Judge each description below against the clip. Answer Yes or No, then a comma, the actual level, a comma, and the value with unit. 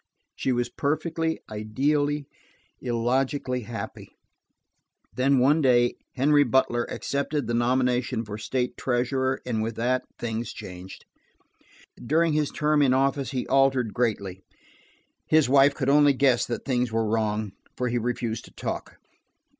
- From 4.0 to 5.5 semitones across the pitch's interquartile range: No, average, 2.9 semitones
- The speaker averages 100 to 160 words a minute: Yes, slow, 135 wpm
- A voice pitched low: Yes, low, 125 Hz